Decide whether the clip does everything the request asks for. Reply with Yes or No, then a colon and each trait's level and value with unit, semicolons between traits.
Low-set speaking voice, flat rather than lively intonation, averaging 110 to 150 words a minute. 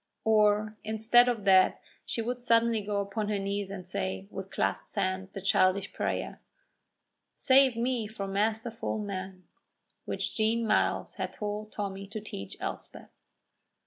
No: high, 210 Hz; narrow, 2.3 semitones; average, 145 wpm